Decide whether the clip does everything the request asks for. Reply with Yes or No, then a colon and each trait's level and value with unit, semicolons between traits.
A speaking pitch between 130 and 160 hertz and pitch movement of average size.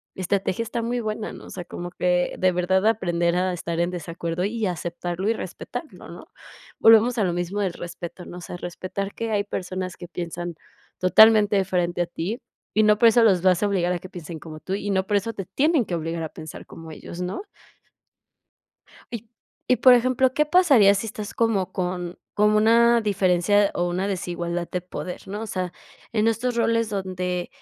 No: high, 190 Hz; average, 3.7 semitones